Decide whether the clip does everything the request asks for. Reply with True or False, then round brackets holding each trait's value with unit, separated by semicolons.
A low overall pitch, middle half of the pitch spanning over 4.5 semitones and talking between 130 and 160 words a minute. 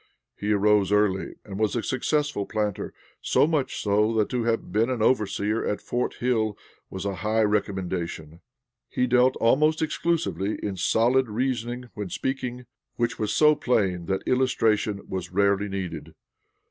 False (110 Hz; 3.9 semitones; 150 wpm)